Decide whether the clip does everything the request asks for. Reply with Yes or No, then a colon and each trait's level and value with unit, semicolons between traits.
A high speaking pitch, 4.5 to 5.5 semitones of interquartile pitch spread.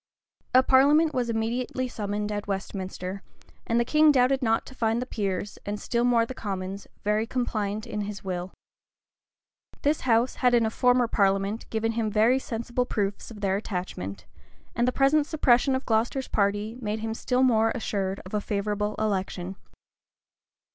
No: high, 225 Hz; average, 3.5 semitones